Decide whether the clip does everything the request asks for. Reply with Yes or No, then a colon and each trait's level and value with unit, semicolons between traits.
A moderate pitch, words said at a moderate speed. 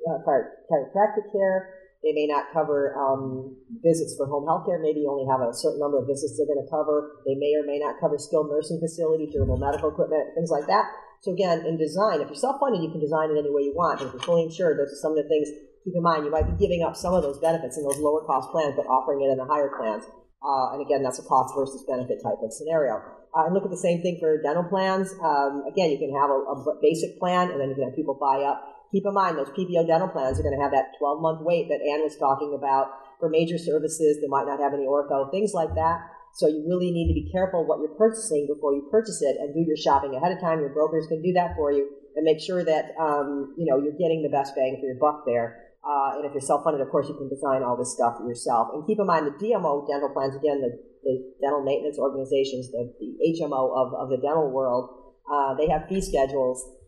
No: medium, 150 Hz; fast, 260 wpm